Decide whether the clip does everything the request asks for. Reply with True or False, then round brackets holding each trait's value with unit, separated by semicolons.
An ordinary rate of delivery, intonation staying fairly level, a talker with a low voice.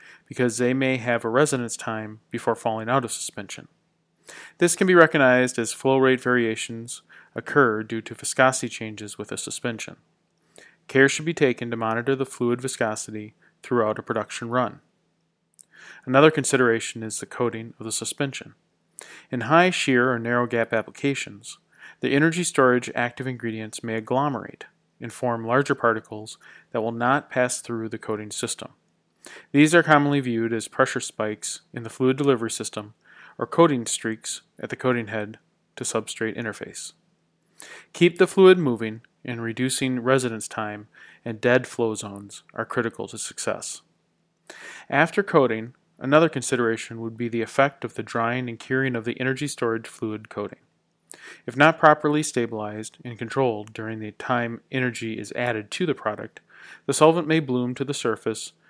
False (155 wpm; 3.2 semitones; 120 Hz)